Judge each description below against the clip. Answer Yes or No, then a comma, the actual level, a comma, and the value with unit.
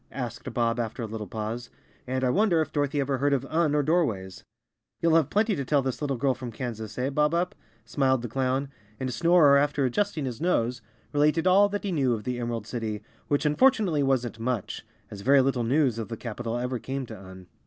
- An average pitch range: Yes, average, 4.1 semitones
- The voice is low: Yes, low, 130 Hz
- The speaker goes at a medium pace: No, fast, 220 wpm